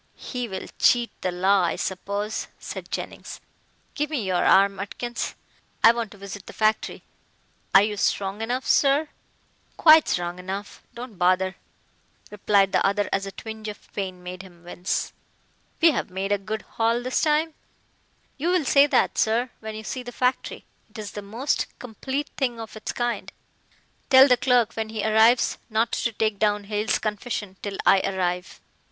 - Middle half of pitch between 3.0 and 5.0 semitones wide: Yes, average, 3.8 semitones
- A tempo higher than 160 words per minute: Yes, average, 170 wpm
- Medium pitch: No, high, 215 Hz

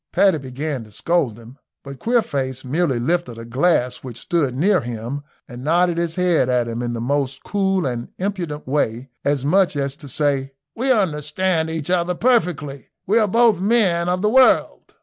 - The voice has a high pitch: No, medium, 150 Hz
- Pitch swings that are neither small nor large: No, wide, 5.7 semitones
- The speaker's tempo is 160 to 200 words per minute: Yes, average, 180 wpm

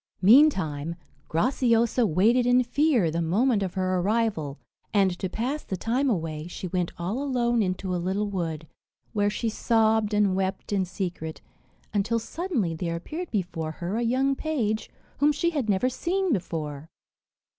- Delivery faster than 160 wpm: No, average, 155 wpm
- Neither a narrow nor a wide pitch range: No, wide, 5.8 semitones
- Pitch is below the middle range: No, high, 205 Hz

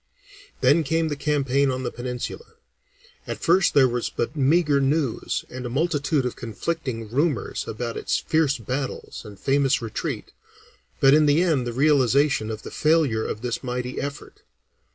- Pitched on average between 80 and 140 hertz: Yes, low, 135 Hz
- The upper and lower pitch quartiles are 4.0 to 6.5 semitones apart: No, average, 3.5 semitones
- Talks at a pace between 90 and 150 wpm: No, average, 160 wpm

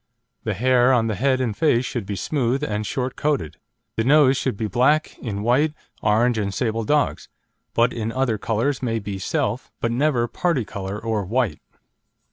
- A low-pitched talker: Yes, low, 120 Hz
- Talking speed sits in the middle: Yes, average, 180 wpm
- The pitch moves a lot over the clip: No, average, 3.6 semitones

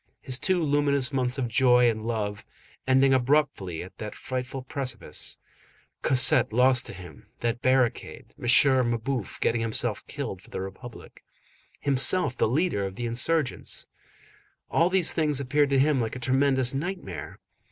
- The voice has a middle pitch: No, low, 130 Hz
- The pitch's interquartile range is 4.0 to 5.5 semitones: No, average, 3.3 semitones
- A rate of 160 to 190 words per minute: No, average, 145 wpm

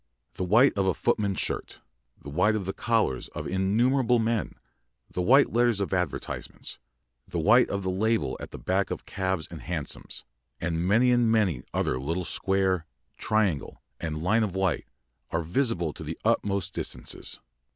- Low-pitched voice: Yes, very low, 95 Hz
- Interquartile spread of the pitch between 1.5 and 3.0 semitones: No, average, 4.3 semitones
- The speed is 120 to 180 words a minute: Yes, average, 165 wpm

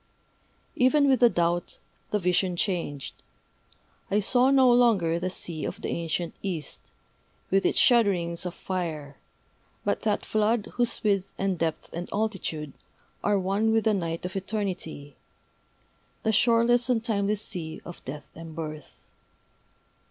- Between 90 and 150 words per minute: Yes, average, 140 wpm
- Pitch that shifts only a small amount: No, average, 4.7 semitones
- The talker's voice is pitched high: Yes, high, 195 Hz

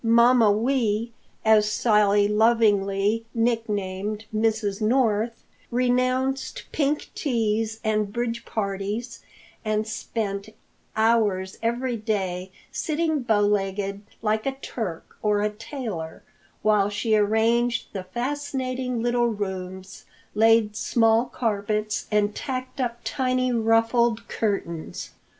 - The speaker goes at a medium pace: No, slow, 105 wpm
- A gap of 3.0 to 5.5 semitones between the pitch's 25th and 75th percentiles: No, narrow, 2.5 semitones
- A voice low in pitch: No, high, 220 Hz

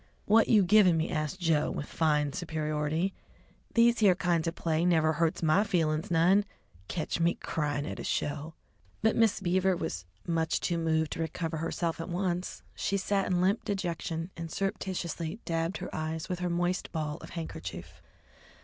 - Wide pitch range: No, narrow, 2.6 semitones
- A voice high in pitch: No, medium, 165 Hz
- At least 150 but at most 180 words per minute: Yes, average, 175 wpm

